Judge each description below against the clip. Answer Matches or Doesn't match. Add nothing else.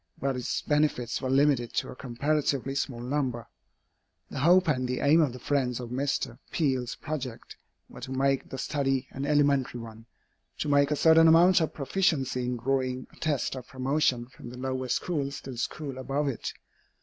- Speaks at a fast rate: Doesn't match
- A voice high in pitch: Doesn't match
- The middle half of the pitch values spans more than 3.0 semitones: Doesn't match